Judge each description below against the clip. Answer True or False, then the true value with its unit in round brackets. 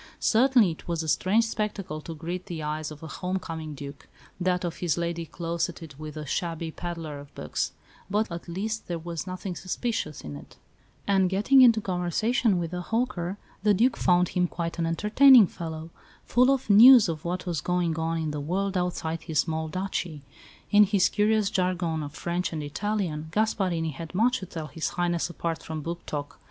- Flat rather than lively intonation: False (3.7 semitones)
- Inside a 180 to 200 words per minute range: True (190 wpm)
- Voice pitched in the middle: True (175 Hz)